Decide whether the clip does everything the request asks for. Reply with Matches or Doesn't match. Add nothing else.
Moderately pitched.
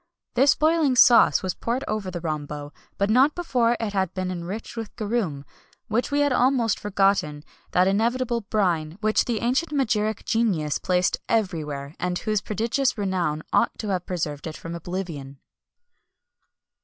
Doesn't match